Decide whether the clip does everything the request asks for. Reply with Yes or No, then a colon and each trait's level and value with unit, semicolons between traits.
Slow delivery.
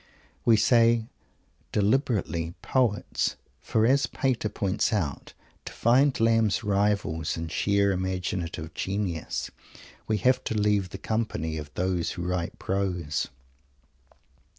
Yes: slow, 115 wpm